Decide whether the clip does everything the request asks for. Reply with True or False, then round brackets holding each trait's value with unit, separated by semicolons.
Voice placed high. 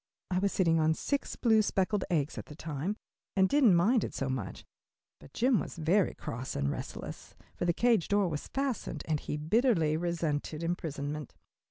False (170 Hz)